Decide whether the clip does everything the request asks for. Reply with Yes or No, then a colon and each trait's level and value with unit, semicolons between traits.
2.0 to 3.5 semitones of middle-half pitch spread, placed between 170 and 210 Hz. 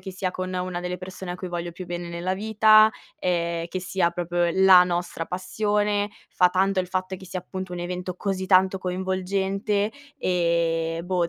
No: narrow, 1.4 semitones; medium, 185 Hz